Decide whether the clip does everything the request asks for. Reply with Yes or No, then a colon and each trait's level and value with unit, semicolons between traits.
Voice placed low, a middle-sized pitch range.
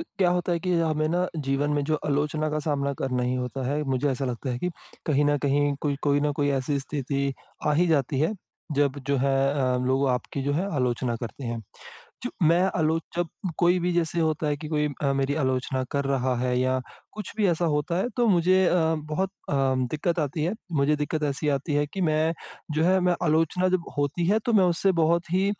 No: medium, 150 Hz; average, 3.6 semitones